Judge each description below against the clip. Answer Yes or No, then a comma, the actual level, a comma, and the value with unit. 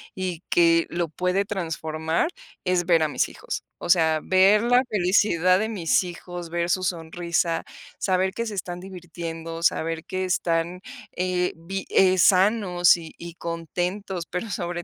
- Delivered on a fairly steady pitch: Yes, narrow, 2.0 semitones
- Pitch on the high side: No, medium, 175 Hz